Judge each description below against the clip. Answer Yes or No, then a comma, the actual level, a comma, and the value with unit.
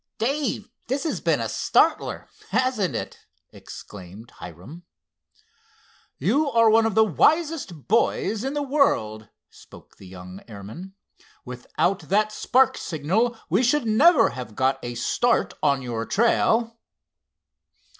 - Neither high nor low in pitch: No, high, 205 Hz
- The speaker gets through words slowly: Yes, slow, 125 wpm